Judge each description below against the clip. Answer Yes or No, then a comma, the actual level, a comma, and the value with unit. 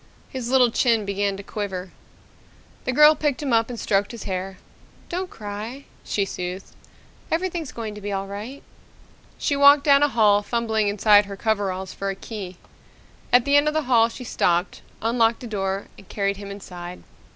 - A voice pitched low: No, high, 215 Hz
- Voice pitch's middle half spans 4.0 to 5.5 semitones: Yes, average, 4.3 semitones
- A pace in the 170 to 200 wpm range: Yes, average, 180 wpm